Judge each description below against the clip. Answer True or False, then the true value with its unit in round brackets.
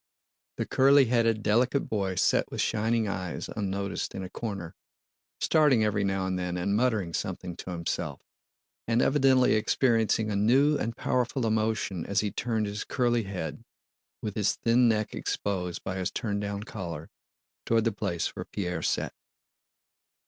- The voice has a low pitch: True (105 Hz)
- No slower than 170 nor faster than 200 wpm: False (155 wpm)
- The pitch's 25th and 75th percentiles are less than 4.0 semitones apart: True (3.5 semitones)